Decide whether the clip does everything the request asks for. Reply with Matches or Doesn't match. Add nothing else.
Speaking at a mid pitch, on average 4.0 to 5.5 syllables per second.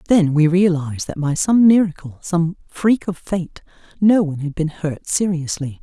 Matches